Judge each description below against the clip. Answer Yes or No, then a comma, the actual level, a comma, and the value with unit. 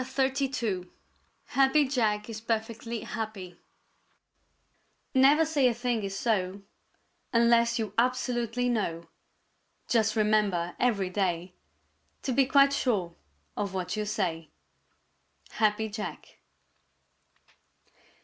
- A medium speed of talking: No, slow, 100 wpm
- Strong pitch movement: No, average, 4.0 semitones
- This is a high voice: Yes, high, 220 Hz